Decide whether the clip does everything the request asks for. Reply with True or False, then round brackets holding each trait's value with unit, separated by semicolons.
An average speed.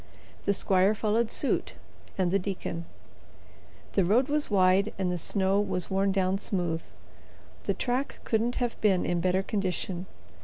True (150 wpm)